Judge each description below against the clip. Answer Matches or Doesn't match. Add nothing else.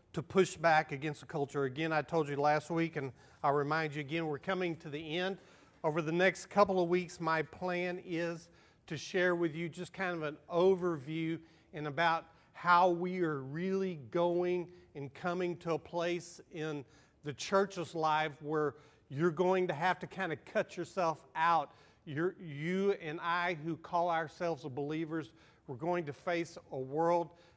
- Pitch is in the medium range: Matches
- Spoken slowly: Doesn't match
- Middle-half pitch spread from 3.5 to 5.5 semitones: Doesn't match